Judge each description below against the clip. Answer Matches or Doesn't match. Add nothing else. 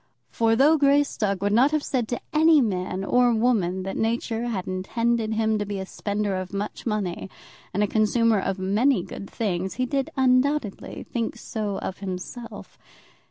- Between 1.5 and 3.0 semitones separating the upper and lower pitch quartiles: Doesn't match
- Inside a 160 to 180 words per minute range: Matches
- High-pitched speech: Matches